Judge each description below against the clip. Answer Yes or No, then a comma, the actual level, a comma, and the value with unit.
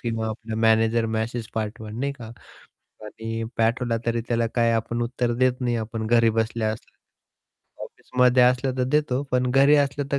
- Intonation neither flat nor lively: No, narrow, 2.0 semitones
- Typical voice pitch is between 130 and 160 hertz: No, low, 115 Hz